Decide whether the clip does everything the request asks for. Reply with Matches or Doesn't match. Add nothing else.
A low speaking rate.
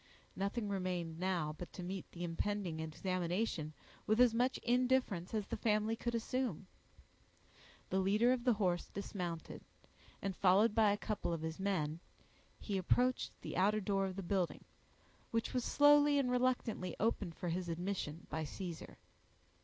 Doesn't match